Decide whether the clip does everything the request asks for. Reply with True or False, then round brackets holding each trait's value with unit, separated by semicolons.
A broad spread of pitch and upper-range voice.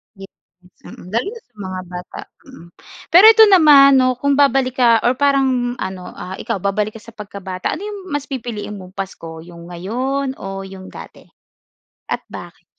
True (6.4 semitones; 230 Hz)